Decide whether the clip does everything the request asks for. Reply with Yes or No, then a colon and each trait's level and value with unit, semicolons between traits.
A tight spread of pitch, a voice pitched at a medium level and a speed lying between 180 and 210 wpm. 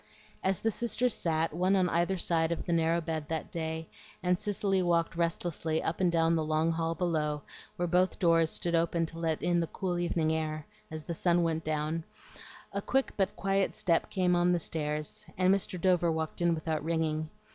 Yes: narrow, 1.9 semitones; medium, 165 Hz; average, 195 wpm